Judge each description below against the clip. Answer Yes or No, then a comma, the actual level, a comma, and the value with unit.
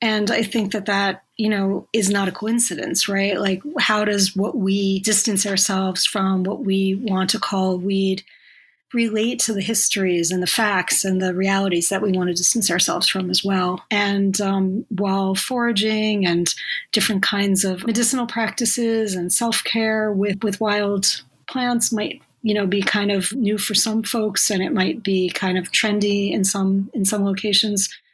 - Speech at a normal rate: Yes, average, 180 wpm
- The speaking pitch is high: Yes, high, 200 Hz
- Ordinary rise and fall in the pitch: No, narrow, 2.1 semitones